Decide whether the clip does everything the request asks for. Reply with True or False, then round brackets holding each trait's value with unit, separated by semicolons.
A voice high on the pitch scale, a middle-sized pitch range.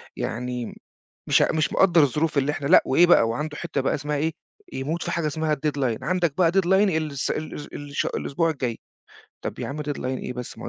False (150 Hz; 3.1 semitones)